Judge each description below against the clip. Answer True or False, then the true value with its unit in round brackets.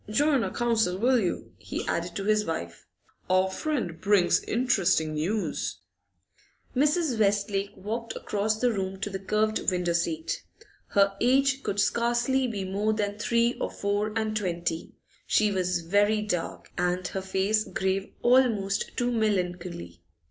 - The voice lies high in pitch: True (205 Hz)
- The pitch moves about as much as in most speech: True (3.6 semitones)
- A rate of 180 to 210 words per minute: False (145 wpm)